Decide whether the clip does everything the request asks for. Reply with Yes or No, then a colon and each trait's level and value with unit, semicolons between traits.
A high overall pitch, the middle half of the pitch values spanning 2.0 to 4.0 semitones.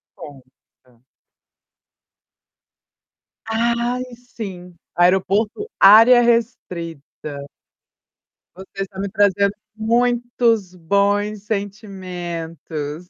No: high, 200 Hz; average, 4.4 semitones